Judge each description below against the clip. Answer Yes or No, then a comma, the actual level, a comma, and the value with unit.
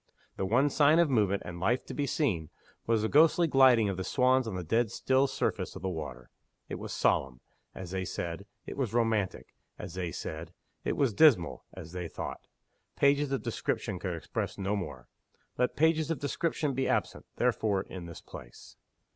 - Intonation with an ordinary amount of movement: No, wide, 7.1 semitones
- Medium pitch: No, low, 110 Hz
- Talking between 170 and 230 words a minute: Yes, average, 190 wpm